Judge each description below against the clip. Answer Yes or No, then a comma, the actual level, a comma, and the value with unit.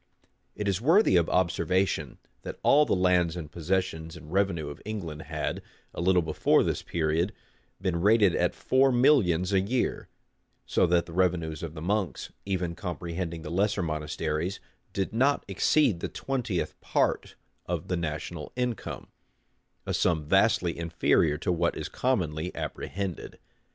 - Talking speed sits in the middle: Yes, average, 150 wpm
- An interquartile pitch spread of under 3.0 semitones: No, average, 3.3 semitones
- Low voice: Yes, very low, 90 Hz